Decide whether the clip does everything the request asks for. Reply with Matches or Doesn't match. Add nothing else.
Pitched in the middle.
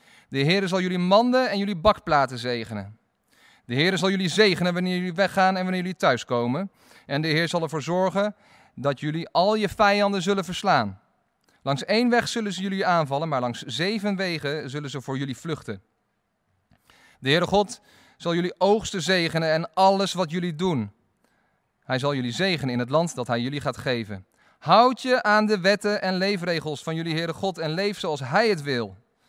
Matches